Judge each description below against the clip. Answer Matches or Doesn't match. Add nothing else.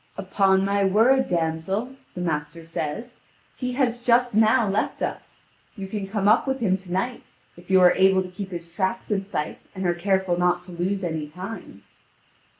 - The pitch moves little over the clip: Doesn't match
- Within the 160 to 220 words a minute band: Matches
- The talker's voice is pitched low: Doesn't match